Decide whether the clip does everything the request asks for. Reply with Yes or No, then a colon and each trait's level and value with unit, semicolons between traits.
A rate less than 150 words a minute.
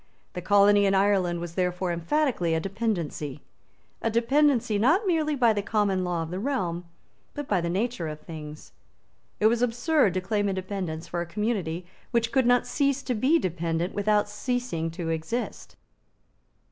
No: average, 165 wpm